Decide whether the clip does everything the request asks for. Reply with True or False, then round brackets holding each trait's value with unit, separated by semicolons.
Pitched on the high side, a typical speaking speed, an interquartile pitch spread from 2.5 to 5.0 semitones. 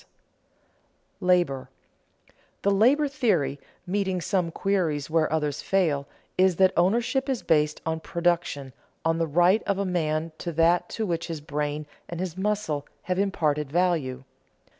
False (170 Hz; 145 wpm; 4.1 semitones)